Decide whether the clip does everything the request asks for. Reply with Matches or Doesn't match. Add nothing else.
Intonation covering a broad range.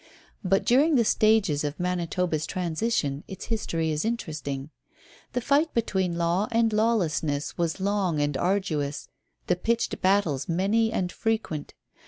Matches